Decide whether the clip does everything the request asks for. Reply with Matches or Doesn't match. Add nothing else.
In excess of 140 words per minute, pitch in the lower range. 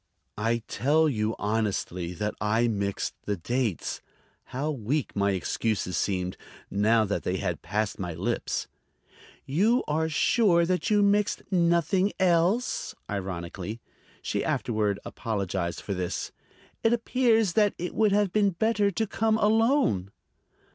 Doesn't match